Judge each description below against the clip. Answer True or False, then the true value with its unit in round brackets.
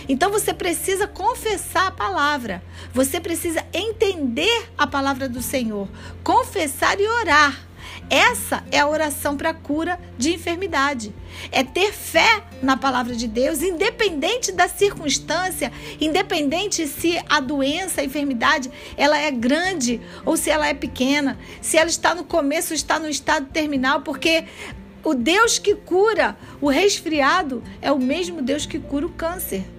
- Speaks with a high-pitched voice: True (315 Hz)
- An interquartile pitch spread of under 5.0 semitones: True (4.4 semitones)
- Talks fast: False (145 wpm)